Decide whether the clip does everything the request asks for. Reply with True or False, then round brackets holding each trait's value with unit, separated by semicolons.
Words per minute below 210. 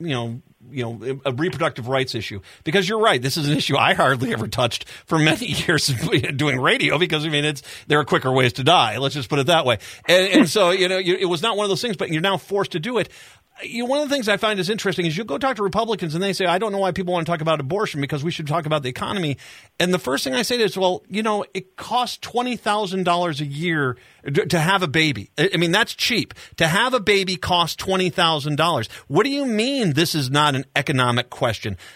False (255 wpm)